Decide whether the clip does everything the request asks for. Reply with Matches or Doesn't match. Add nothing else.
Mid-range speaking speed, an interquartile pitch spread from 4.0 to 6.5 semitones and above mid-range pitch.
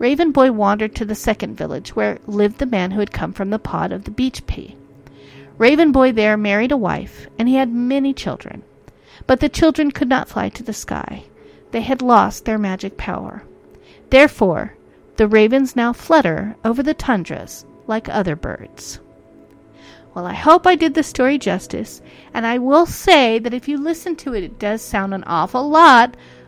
Matches